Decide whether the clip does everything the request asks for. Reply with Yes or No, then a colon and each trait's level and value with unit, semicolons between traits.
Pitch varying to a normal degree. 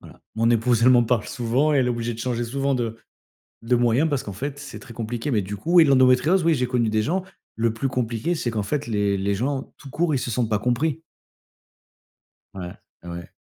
Yes: average, 3.6 semitones